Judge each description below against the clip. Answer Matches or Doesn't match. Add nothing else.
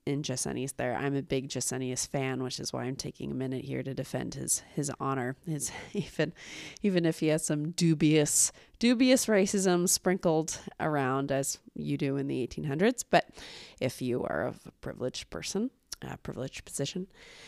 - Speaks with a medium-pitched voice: Matches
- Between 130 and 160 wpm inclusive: Doesn't match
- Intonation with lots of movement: Doesn't match